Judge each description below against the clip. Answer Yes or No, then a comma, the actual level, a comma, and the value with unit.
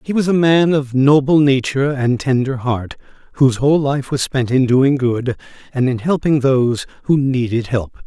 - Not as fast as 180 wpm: No, average, 185 wpm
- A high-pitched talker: No, low, 135 Hz